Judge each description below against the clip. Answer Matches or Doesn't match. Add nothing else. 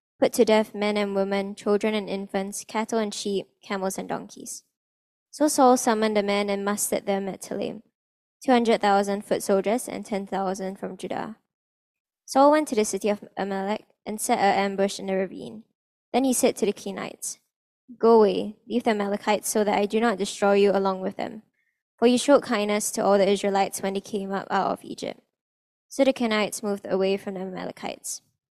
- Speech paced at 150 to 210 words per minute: Matches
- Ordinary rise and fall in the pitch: Doesn't match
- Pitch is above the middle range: Matches